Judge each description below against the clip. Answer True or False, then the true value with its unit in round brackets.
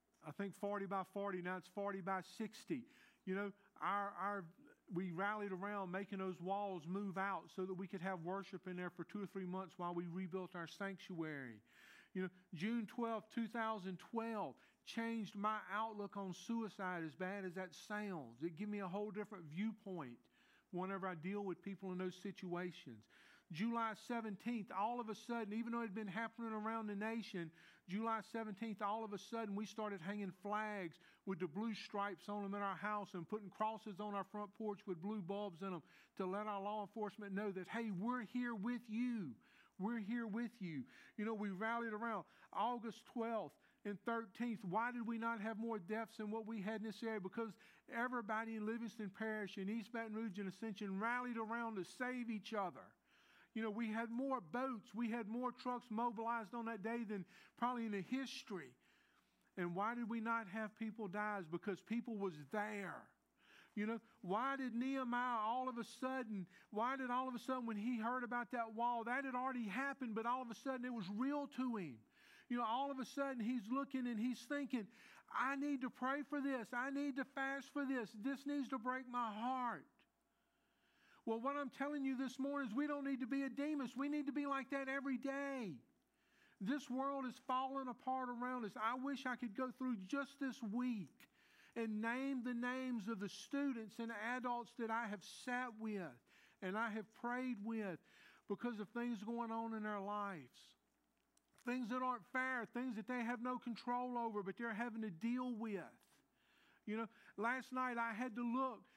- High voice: True (225 Hz)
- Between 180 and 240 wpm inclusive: True (200 wpm)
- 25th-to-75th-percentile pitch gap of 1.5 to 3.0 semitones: False (3.5 semitones)